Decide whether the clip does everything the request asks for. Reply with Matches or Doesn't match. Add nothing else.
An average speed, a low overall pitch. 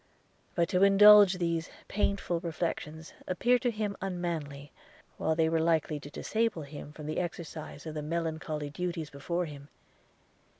Doesn't match